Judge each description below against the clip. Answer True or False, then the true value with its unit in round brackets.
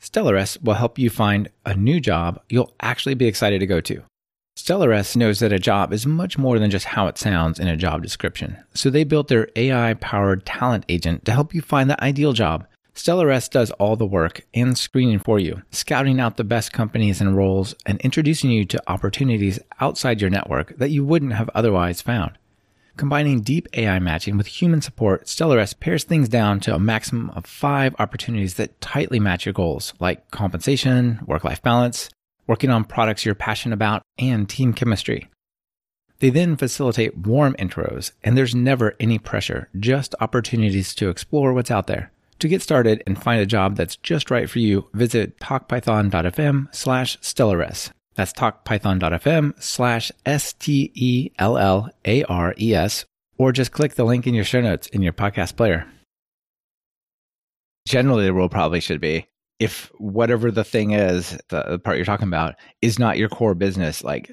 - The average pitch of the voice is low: True (110 Hz)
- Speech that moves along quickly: False (180 wpm)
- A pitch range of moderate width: True (4.6 semitones)